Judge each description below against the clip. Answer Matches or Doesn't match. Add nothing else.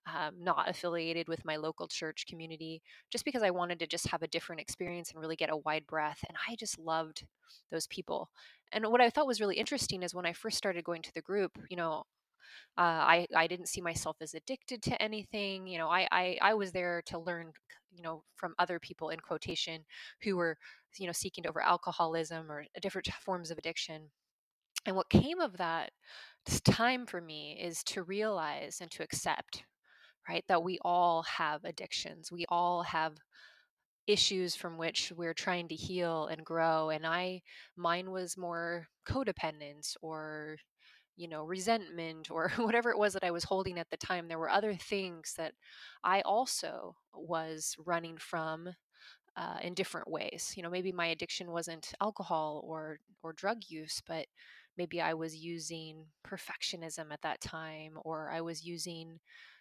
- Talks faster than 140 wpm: Matches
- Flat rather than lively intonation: Matches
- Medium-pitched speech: Matches